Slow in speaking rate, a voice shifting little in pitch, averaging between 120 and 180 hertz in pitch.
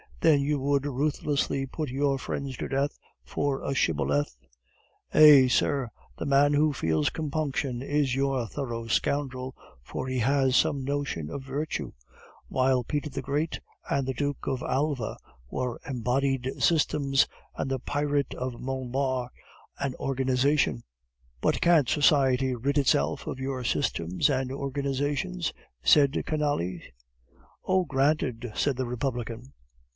Yes: slow, 130 wpm; narrow, 2.1 semitones; low, 135 Hz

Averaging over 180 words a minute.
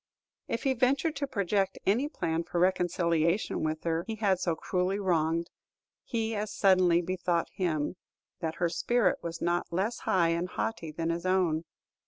No: average, 165 wpm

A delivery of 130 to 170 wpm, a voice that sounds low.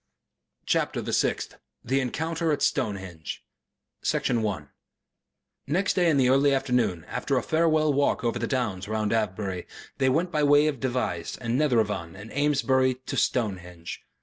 Yes: average, 150 wpm; low, 125 Hz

